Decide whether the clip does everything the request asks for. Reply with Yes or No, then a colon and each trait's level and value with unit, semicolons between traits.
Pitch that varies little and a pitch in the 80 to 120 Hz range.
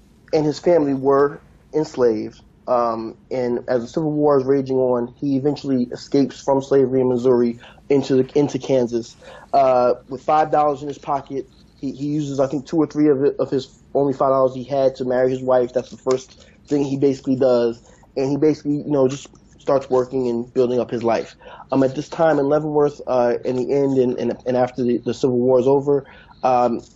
No: narrow, 2.2 semitones; low, 135 Hz